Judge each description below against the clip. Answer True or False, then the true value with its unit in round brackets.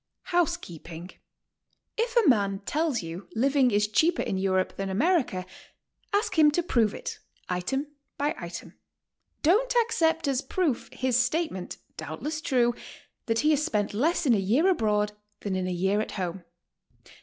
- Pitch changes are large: True (8.6 semitones)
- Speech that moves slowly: False (155 wpm)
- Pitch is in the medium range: False (245 Hz)